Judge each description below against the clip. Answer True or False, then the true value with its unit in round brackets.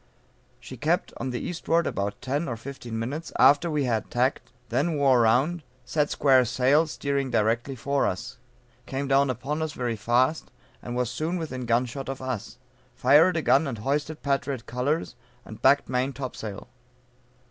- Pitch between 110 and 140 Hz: True (135 Hz)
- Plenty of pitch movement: False (3.1 semitones)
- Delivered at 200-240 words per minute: False (170 wpm)